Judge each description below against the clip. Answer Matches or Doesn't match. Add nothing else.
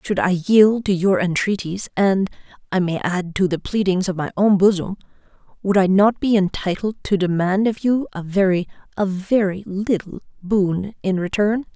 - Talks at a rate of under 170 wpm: Matches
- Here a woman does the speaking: Matches